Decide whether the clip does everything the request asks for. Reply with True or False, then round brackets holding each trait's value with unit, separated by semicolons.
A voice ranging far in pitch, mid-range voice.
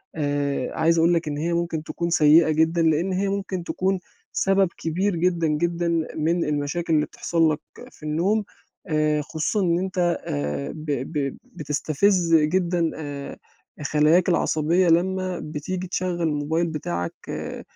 False (2.7 semitones; 165 Hz)